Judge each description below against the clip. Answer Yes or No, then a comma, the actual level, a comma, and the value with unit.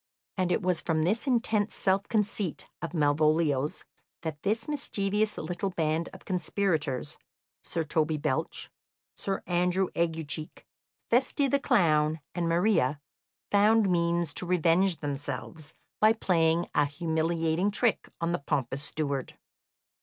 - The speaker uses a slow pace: Yes, slow, 125 wpm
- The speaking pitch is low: No, medium, 170 Hz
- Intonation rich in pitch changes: No, average, 4.1 semitones